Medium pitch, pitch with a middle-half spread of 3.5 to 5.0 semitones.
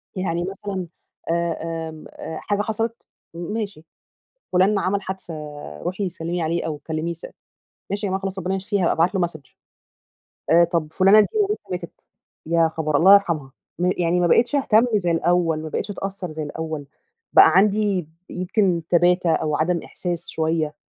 No: medium, 175 Hz; average, 3.1 semitones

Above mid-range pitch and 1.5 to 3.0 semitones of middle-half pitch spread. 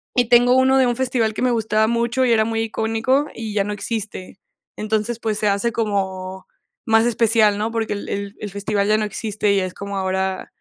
Yes: high, 220 Hz; narrow, 2.5 semitones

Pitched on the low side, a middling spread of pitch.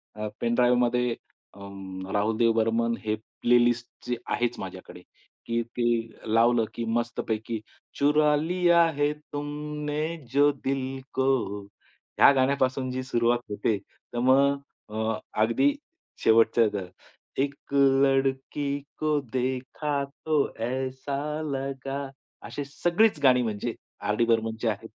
Yes: low, 125 Hz; average, 3.6 semitones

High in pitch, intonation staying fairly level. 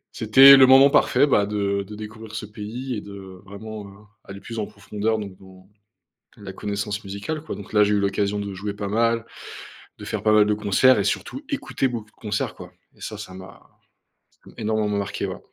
No: low, 105 Hz; narrow, 1.8 semitones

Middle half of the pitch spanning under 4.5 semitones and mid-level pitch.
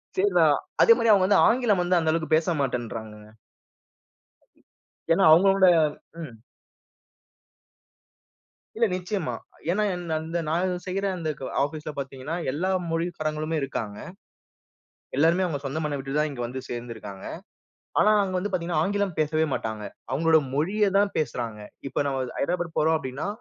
No: average, 5.1 semitones; medium, 160 Hz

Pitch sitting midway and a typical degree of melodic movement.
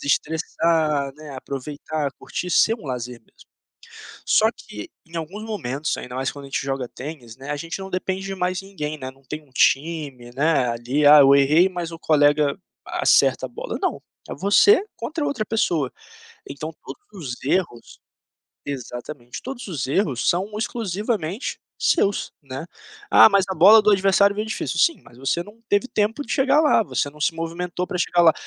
No: medium, 160 Hz; wide, 6.0 semitones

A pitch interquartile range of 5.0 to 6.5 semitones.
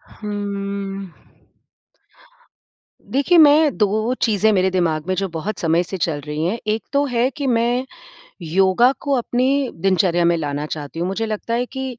Yes: wide, 5.5 semitones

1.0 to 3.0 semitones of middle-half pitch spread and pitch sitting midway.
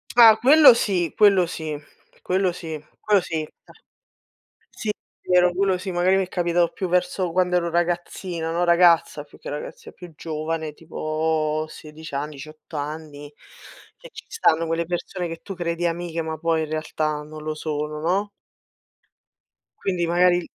Yes: narrow, 2.6 semitones; medium, 170 Hz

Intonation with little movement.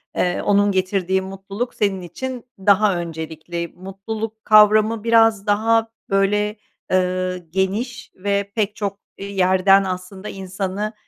Yes: narrow, 2.2 semitones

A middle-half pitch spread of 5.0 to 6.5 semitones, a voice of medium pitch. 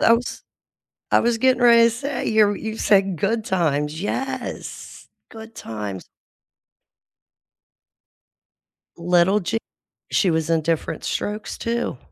No: wide, 5.6 semitones; high, 210 Hz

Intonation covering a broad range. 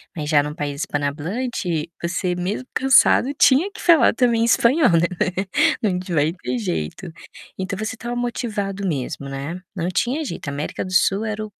Yes: wide, 7.8 semitones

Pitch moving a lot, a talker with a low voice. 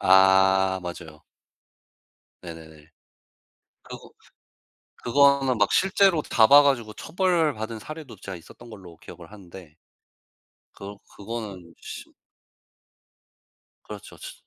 Yes: wide, 7.4 semitones; low, 105 Hz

